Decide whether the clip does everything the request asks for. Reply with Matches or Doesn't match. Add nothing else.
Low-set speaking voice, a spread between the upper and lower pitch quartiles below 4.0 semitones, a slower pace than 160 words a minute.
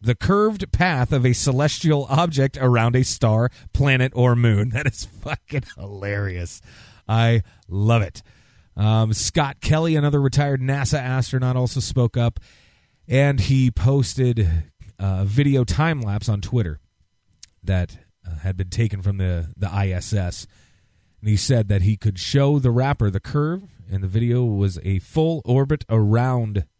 Doesn't match